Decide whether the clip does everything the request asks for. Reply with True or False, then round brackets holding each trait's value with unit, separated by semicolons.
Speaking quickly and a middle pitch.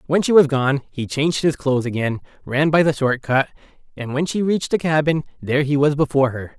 True (230 wpm; 145 Hz)